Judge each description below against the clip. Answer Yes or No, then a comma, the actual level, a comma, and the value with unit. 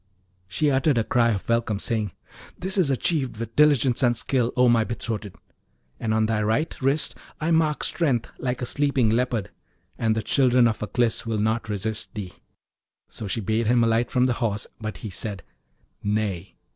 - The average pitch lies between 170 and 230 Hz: No, low, 115 Hz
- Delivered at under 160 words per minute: No, average, 180 wpm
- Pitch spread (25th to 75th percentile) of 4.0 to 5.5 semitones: No, average, 2.9 semitones